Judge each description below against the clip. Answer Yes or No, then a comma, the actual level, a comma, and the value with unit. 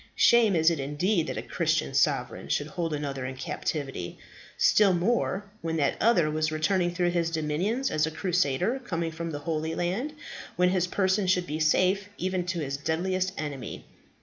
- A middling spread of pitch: Yes, average, 3.4 semitones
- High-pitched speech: No, medium, 170 Hz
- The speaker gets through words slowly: No, average, 175 wpm